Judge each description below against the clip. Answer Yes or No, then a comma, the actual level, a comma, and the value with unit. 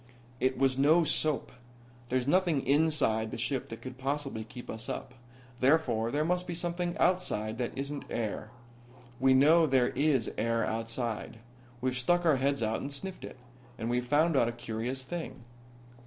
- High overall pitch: No, low, 135 Hz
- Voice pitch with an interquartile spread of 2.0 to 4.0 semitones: No, average, 4.8 semitones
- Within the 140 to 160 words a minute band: No, average, 170 wpm